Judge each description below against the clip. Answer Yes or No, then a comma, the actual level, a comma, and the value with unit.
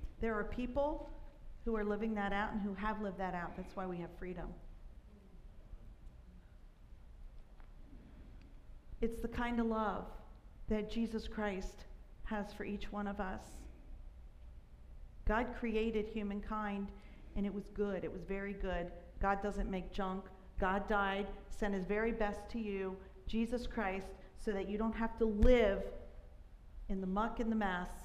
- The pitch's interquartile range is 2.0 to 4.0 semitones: Yes, average, 2.9 semitones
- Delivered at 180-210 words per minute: No, average, 150 wpm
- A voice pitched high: Yes, high, 200 Hz